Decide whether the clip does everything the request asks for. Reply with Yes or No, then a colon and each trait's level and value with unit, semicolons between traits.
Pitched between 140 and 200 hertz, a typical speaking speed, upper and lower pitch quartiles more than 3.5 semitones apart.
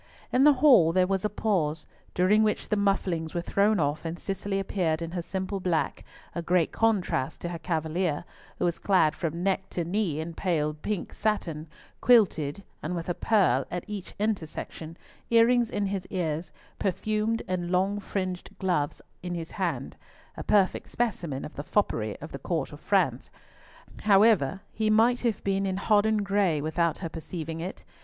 Yes: medium, 185 Hz; average, 170 wpm; average, 4.0 semitones